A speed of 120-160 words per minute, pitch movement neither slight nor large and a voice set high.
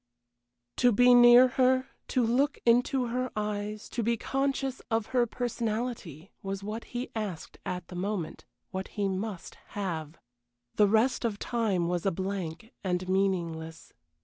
Yes: average, 150 wpm; average, 4.5 semitones; high, 215 Hz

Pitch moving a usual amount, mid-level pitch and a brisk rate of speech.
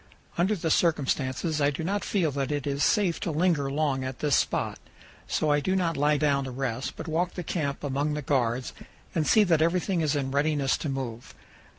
Yes: average, 3.3 semitones; medium, 150 Hz; fast, 210 wpm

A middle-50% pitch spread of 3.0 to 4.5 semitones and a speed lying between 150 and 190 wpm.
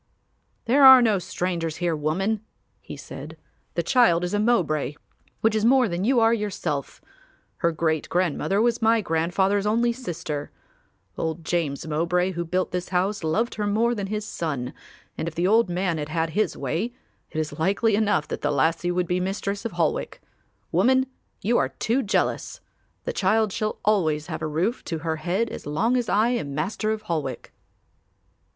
No: average, 5.2 semitones; average, 180 wpm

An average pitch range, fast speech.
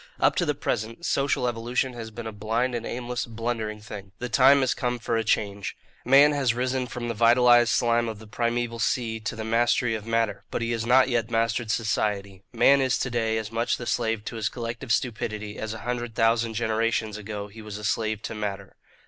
No: narrow, 1.8 semitones; fast, 215 wpm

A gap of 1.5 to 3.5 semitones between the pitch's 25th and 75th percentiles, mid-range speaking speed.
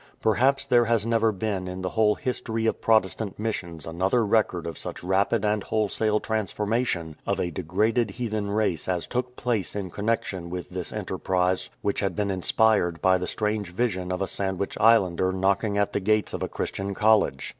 Yes: average, 3.2 semitones; average, 180 wpm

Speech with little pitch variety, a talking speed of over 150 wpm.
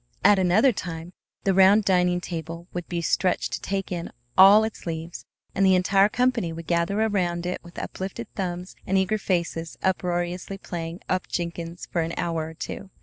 Yes: narrow, 2.3 semitones; average, 180 wpm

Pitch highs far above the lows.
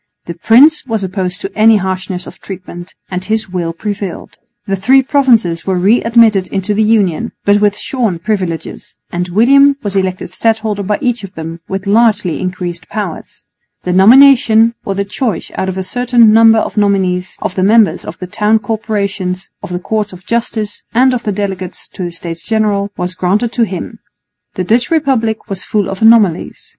No: average, 3.4 semitones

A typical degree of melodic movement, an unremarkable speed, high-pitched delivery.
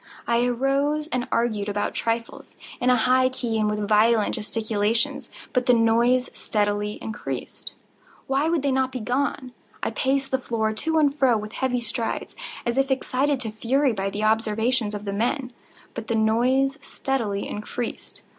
Yes: average, 3.4 semitones; average, 165 wpm; high, 240 Hz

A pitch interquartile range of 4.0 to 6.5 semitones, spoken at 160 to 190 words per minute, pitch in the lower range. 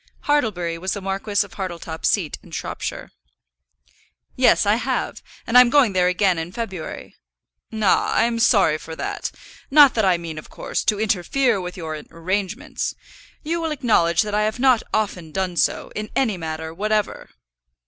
No: average, 4.7 semitones; average, 165 wpm; high, 195 Hz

